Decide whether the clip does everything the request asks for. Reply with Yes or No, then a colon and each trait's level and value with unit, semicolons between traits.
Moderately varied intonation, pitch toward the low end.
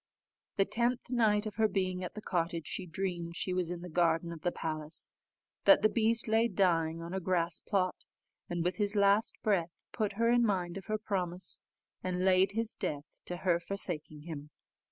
No: average, 3.6 semitones; medium, 185 Hz